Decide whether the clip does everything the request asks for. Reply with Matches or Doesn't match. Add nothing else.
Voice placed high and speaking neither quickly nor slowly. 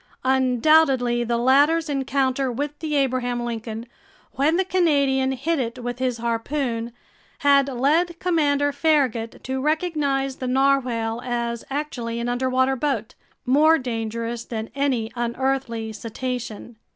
Doesn't match